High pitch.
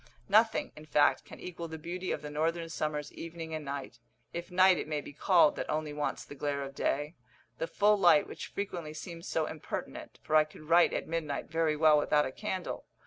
No: medium, 155 Hz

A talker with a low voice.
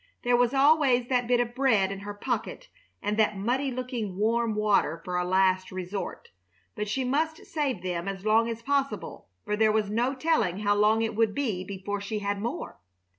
No: high, 220 Hz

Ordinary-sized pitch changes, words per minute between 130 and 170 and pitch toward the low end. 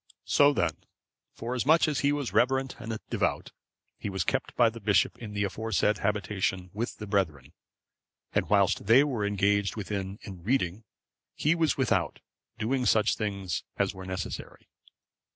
Yes: average, 4.1 semitones; average, 150 wpm; low, 105 Hz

